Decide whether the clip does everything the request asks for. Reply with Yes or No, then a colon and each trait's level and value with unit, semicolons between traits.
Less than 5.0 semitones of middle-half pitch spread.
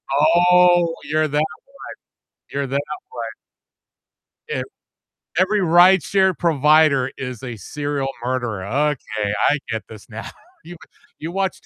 No: average, 5.3 semitones